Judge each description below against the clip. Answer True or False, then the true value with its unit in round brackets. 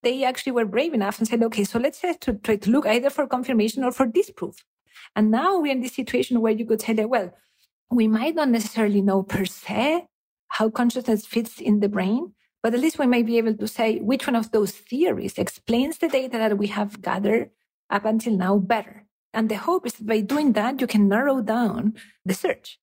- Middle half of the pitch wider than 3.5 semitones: False (3.2 semitones)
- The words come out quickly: True (220 wpm)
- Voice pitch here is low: False (230 Hz)